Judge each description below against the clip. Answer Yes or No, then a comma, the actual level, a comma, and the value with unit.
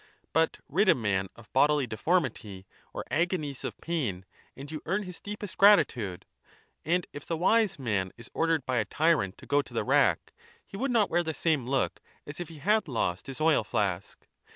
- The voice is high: No, medium, 150 Hz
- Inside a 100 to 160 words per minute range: No, average, 185 wpm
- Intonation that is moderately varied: No, wide, 6.9 semitones